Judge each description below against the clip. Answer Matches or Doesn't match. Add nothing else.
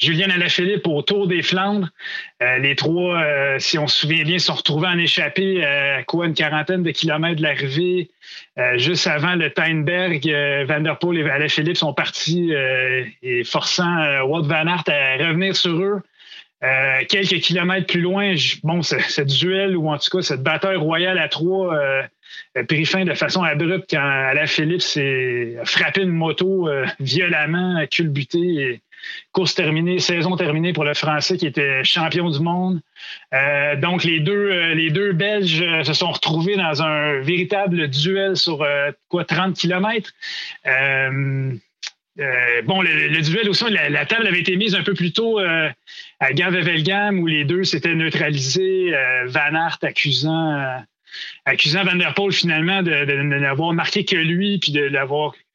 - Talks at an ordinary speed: Matches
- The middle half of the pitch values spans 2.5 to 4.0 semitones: Matches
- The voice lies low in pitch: Doesn't match